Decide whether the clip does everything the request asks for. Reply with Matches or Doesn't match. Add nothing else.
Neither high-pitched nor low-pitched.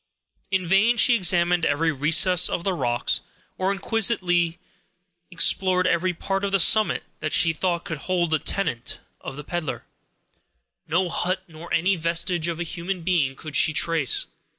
Matches